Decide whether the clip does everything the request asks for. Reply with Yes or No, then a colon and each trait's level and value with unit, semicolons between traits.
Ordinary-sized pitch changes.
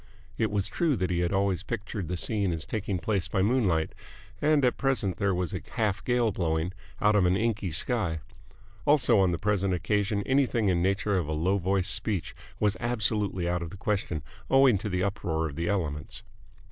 Yes: average, 3.6 semitones